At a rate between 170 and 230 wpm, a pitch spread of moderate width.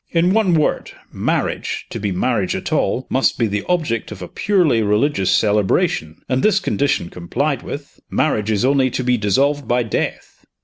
No: average, 175 wpm; wide, 5.9 semitones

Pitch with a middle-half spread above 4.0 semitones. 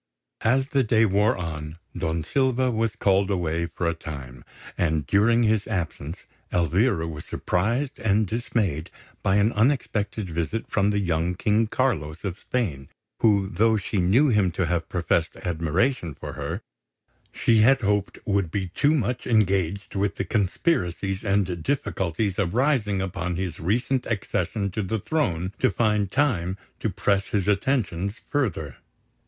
Yes: average, 4.5 semitones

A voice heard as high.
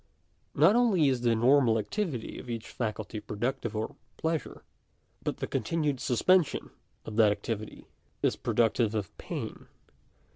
No: low, 120 Hz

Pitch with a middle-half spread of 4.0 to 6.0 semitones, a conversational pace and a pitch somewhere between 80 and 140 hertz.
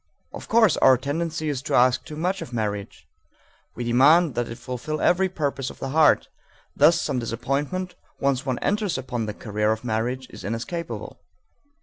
Yes: average, 5.1 semitones; average, 175 wpm; low, 135 Hz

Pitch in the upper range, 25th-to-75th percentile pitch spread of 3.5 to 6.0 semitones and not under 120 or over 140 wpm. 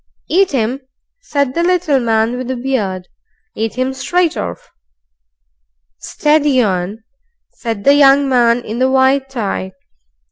Yes: very high, 260 Hz; average, 3.9 semitones; slow, 135 wpm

